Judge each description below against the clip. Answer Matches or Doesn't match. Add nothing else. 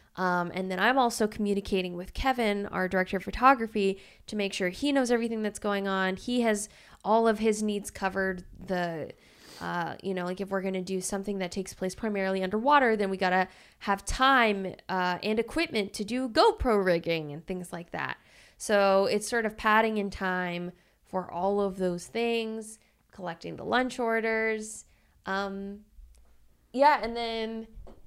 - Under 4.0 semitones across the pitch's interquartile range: Matches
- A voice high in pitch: Matches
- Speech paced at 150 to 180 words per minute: Matches